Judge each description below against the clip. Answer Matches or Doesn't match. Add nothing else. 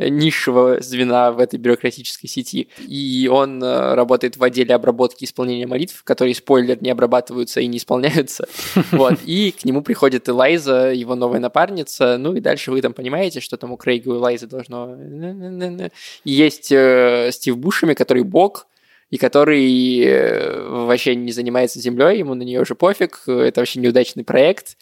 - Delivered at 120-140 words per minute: Doesn't match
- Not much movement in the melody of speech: Matches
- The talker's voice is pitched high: Doesn't match